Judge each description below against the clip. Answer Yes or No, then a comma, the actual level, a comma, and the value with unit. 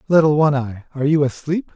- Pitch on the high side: No, medium, 145 Hz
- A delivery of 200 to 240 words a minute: Yes, fast, 205 wpm